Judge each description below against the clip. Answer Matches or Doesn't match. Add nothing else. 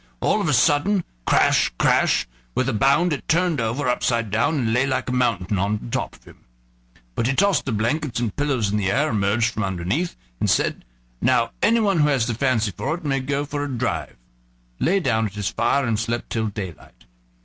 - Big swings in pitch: Doesn't match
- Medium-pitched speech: Doesn't match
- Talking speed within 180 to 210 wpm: Matches